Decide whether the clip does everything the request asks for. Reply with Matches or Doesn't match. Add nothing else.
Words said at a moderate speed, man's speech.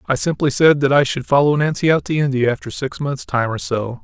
Doesn't match